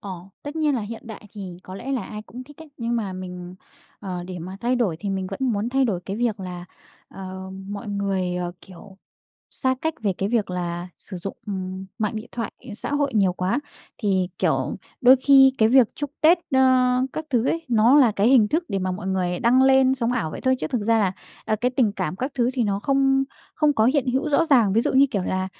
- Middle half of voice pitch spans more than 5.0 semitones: Yes, wide, 5.5 semitones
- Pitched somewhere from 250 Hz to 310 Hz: No, high, 220 Hz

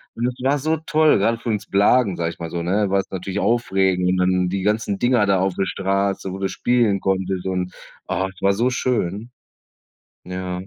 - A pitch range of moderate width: Yes, average, 3.7 semitones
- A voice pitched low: Yes, very low, 95 Hz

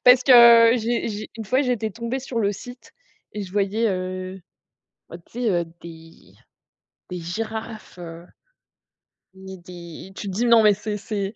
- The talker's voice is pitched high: Yes, high, 210 Hz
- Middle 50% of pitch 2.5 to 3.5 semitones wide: No, average, 4.0 semitones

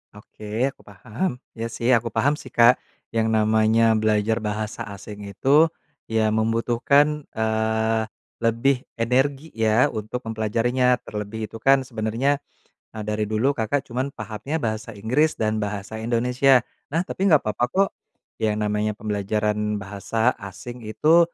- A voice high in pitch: No, low, 110 Hz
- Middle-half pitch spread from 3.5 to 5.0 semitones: No, average, 2.8 semitones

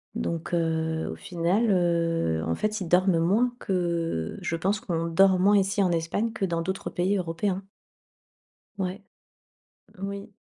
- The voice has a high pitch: No, medium, 180 Hz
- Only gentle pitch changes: No, average, 3.0 semitones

